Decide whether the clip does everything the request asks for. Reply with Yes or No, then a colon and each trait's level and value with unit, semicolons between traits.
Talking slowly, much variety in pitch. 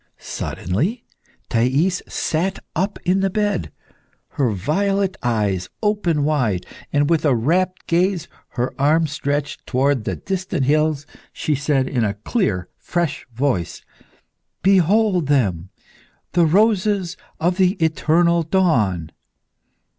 Yes: slow, 120 wpm; wide, 6.4 semitones